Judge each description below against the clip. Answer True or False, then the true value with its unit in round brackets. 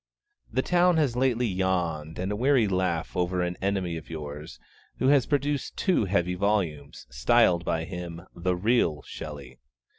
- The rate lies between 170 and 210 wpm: False (150 wpm)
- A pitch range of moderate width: False (6.2 semitones)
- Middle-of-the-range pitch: False (90 Hz)